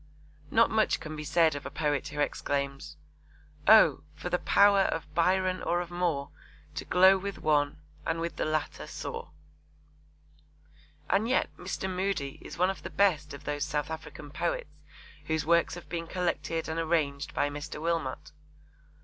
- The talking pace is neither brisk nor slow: Yes, average, 165 wpm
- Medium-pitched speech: Yes, medium, 160 Hz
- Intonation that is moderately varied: Yes, average, 3.5 semitones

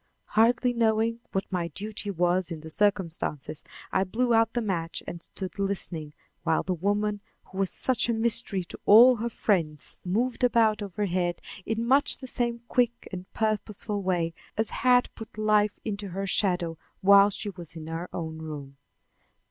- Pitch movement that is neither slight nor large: Yes, average, 4.3 semitones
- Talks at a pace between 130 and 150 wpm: No, average, 165 wpm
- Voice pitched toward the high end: Yes, high, 200 Hz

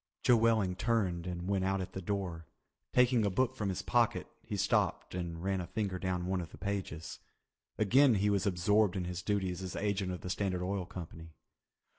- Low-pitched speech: Yes, very low, 95 Hz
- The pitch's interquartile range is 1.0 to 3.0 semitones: Yes, narrow, 2.4 semitones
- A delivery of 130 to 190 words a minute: No, average, 200 wpm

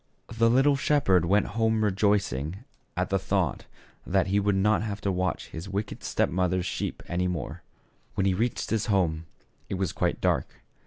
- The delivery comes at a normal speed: Yes, average, 180 wpm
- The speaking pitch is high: No, low, 100 Hz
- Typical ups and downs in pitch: Yes, average, 3.0 semitones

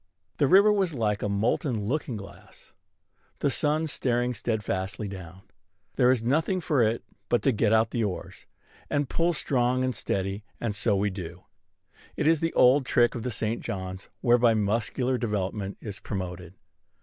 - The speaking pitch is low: Yes, low, 115 Hz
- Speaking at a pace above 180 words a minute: No, average, 165 wpm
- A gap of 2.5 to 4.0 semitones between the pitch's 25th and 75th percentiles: No, average, 4.5 semitones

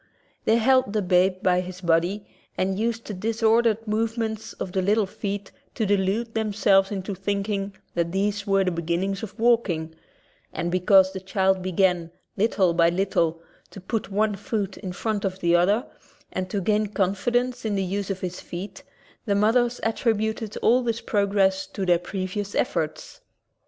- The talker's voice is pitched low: No, high, 200 Hz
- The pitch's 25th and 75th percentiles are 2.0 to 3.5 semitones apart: Yes, average, 2.7 semitones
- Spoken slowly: No, average, 170 wpm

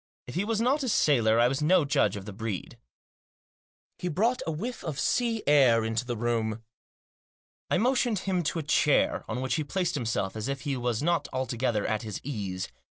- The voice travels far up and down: Yes, wide, 7.8 semitones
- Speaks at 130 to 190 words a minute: No, average, 200 wpm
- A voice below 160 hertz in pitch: Yes, low, 135 Hz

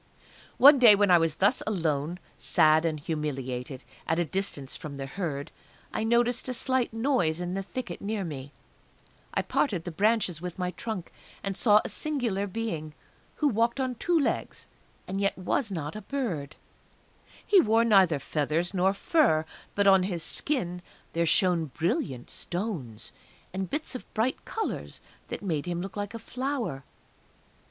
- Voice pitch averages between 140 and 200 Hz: Yes, high, 190 Hz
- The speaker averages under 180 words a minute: Yes, average, 160 wpm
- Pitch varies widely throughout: Yes, wide, 6.2 semitones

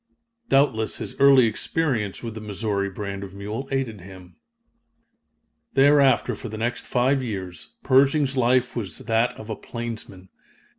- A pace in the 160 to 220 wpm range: No, average, 140 wpm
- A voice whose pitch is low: Yes, low, 115 Hz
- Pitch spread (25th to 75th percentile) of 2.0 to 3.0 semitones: No, average, 4.7 semitones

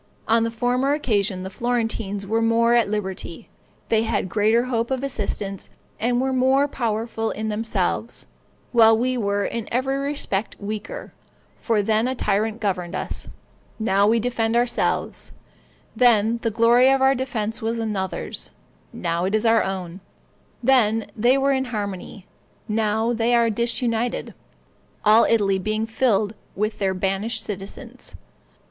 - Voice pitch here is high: Yes, high, 225 Hz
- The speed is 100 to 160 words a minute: Yes, average, 145 wpm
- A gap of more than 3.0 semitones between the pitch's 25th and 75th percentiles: No, average, 2.7 semitones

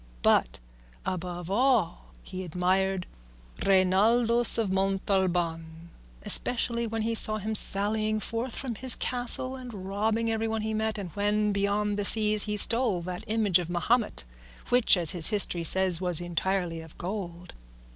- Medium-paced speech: Yes, average, 145 wpm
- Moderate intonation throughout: Yes, average, 3.6 semitones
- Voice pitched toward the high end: Yes, high, 200 Hz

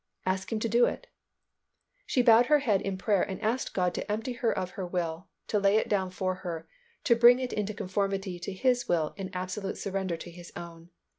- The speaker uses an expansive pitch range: No, average, 3.5 semitones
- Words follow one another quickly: Yes, fast, 215 wpm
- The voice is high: Yes, high, 195 Hz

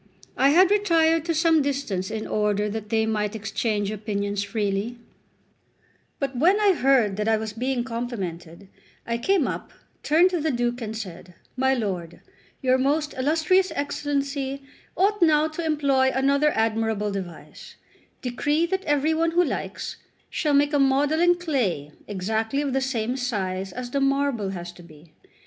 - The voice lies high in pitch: Yes, very high, 255 Hz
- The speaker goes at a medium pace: Yes, average, 160 wpm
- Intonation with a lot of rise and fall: Yes, wide, 6.0 semitones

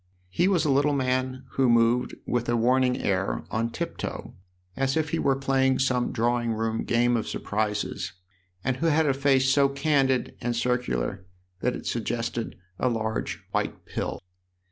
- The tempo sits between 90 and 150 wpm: No, average, 165 wpm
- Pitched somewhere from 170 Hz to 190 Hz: No, low, 125 Hz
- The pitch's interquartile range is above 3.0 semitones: No, narrow, 2.6 semitones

